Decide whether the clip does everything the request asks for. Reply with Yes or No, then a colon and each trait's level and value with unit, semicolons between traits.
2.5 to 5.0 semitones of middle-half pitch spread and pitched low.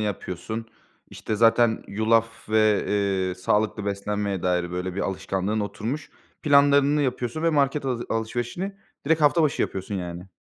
No: wide, 5.6 semitones; low, 110 Hz